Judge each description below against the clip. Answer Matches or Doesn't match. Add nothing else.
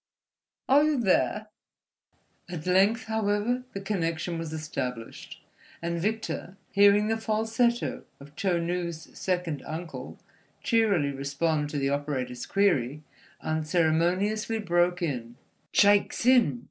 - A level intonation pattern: Doesn't match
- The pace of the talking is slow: Matches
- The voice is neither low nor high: Matches